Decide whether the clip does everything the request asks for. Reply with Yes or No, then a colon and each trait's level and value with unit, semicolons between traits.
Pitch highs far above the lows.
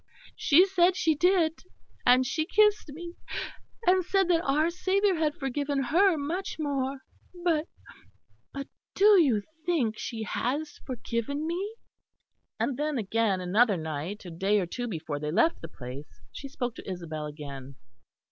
Yes: wide, 8.8 semitones